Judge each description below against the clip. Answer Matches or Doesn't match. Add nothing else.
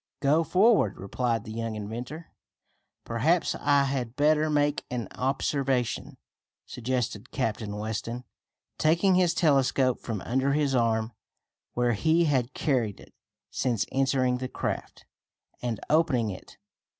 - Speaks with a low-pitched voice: Matches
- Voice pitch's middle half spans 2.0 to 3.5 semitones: Doesn't match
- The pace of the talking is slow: Matches